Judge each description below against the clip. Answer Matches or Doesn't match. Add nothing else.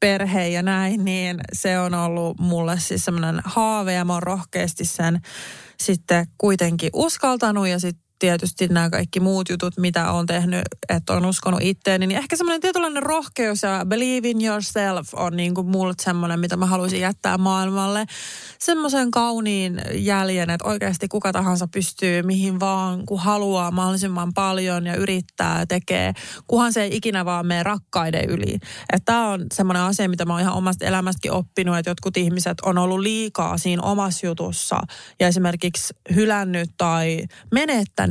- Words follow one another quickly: Matches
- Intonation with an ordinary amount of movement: Doesn't match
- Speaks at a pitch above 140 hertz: Matches